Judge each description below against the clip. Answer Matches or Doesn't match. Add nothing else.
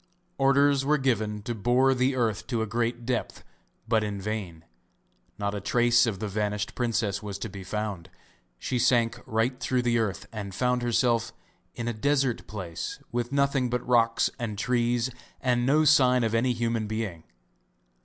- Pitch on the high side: Doesn't match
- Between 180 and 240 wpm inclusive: Doesn't match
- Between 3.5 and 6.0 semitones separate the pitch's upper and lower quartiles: Doesn't match